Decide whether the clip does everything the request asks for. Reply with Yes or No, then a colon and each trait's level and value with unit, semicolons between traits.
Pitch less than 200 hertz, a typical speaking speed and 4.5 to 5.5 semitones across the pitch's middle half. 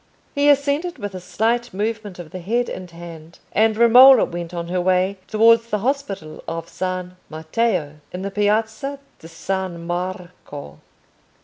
Yes: high, 190 Hz; average, 150 wpm; average, 4.8 semitones